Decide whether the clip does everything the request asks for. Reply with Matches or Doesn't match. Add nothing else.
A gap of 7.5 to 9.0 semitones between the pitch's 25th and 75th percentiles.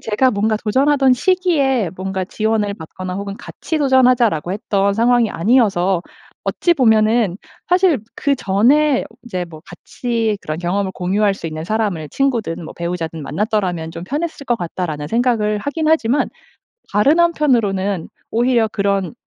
Doesn't match